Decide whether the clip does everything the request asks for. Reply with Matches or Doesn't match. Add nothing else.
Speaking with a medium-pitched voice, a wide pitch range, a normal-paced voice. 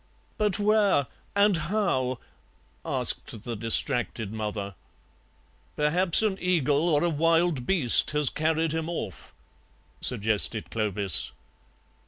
Doesn't match